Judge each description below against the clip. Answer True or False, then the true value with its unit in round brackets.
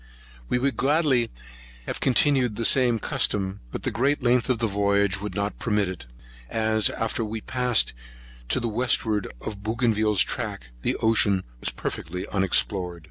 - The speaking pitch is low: True (110 Hz)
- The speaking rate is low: False (160 wpm)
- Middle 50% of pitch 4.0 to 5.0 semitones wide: False (3.4 semitones)